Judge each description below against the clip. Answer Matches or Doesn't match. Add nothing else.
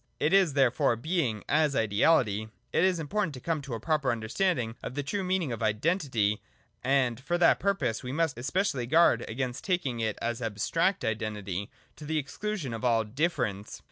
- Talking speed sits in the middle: Matches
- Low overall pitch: Matches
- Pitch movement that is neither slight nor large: Doesn't match